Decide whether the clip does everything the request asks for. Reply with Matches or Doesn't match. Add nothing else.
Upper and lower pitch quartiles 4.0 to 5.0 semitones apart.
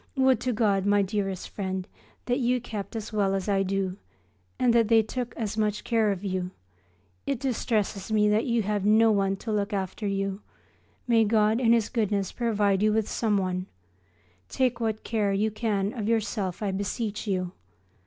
Doesn't match